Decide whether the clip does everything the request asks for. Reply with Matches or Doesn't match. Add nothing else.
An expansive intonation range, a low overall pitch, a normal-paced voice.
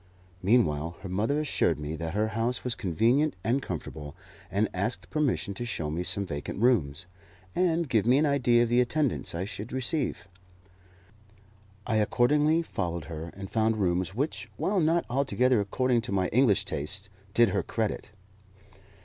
Matches